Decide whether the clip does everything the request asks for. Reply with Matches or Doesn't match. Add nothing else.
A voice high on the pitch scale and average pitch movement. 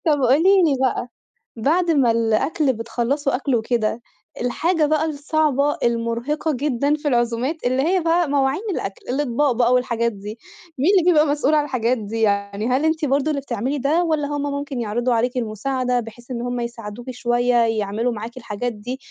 Matches